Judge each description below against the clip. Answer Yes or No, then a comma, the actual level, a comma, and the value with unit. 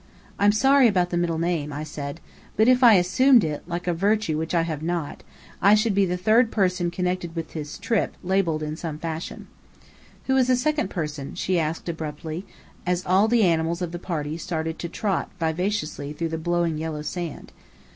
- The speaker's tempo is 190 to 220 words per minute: Yes, average, 195 wpm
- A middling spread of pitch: Yes, average, 3.7 semitones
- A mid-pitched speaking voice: Yes, medium, 175 Hz